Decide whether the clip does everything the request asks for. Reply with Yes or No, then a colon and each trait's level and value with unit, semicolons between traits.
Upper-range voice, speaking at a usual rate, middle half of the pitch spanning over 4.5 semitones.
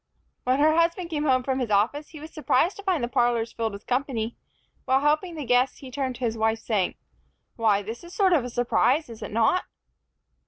No: very high, 255 Hz; fast, 220 wpm; average, 5.0 semitones